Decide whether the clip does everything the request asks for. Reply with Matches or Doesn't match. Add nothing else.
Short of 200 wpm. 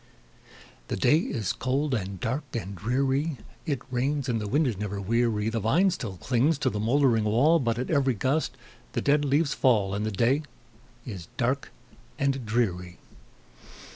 Matches